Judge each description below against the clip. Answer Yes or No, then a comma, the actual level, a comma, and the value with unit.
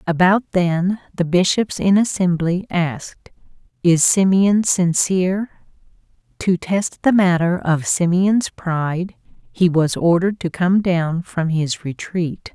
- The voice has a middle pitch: Yes, medium, 180 Hz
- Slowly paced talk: Yes, slow, 125 wpm